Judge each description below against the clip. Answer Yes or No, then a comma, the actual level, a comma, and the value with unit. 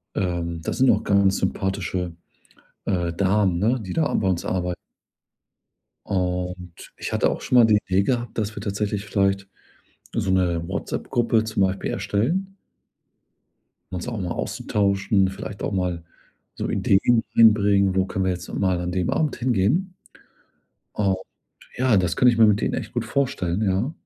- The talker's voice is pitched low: Yes, low, 100 Hz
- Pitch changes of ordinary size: Yes, average, 3.2 semitones